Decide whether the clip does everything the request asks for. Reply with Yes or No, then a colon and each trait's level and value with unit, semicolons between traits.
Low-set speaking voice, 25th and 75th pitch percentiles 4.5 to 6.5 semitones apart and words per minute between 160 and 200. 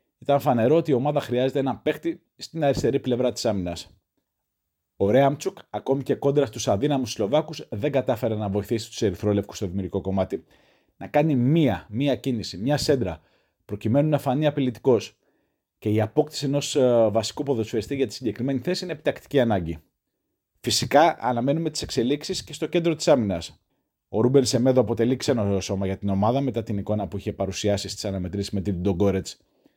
Yes: low, 125 Hz; wide, 5.6 semitones; average, 165 wpm